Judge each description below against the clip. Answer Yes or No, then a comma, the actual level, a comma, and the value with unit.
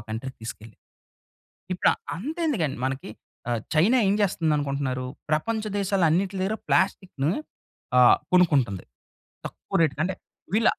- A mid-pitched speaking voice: Yes, medium, 160 Hz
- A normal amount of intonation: No, wide, 6.9 semitones